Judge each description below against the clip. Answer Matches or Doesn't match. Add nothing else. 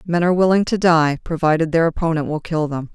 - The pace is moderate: Doesn't match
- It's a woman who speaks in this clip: Matches